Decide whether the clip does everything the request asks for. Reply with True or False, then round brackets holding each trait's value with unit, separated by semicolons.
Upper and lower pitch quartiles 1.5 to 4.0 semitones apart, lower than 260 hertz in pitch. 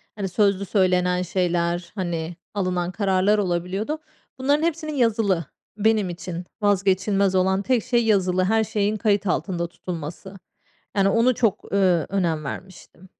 True (2.8 semitones; 190 Hz)